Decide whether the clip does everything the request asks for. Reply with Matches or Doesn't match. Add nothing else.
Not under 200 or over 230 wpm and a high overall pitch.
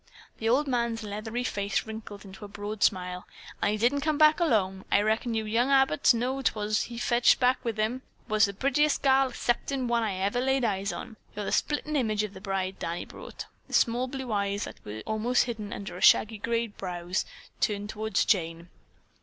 Matches